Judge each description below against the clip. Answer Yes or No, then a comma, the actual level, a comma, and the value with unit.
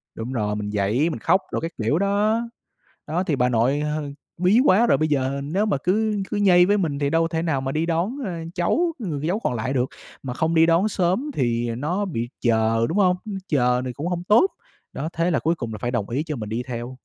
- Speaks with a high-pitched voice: No, medium, 155 Hz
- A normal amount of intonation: No, wide, 6.7 semitones